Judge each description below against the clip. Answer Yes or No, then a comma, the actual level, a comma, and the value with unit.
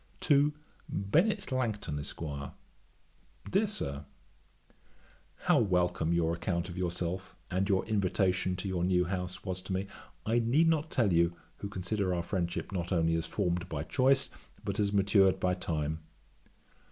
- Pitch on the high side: No, very low, 95 Hz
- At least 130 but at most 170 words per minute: Yes, average, 150 wpm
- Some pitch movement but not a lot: Yes, average, 3.3 semitones